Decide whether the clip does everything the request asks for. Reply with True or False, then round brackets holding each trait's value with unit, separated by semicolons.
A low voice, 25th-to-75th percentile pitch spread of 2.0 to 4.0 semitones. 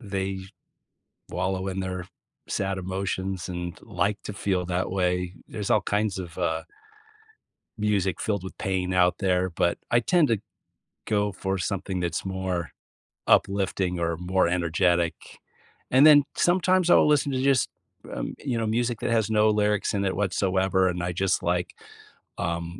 True (95 Hz; 2.7 semitones)